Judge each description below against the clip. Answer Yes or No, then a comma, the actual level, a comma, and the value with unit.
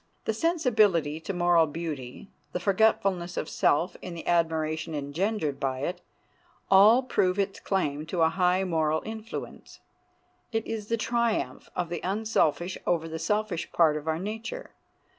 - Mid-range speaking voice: Yes, medium, 175 Hz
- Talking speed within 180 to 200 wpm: No, average, 150 wpm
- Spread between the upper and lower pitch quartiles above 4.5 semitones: Yes, average, 4.9 semitones